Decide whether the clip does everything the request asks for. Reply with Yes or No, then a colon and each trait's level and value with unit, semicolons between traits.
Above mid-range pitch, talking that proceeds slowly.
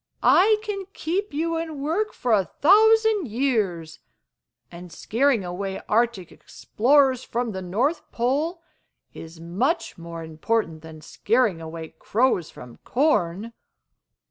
Yes: high, 235 Hz; slow, 120 wpm